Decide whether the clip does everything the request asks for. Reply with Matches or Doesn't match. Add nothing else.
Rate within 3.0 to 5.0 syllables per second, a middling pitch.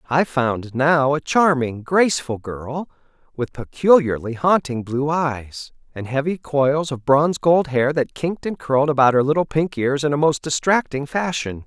Matches